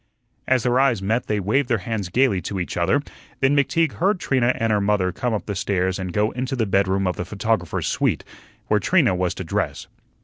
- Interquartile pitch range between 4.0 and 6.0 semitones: Yes, average, 5.1 semitones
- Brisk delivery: Yes, fast, 215 wpm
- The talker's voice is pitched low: Yes, low, 105 Hz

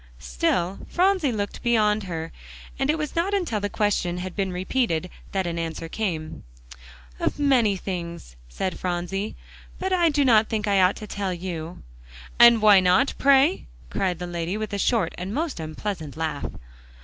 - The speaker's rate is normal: Yes, average, 170 wpm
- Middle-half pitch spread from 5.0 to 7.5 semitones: Yes, wide, 5.4 semitones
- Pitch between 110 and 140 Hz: No, high, 195 Hz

